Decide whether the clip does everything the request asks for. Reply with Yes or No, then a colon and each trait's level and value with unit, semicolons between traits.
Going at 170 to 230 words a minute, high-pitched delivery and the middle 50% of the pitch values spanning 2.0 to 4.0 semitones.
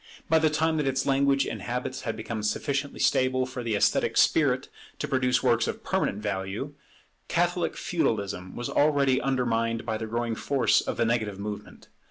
No: average, 175 wpm; low, 120 Hz; average, 3.7 semitones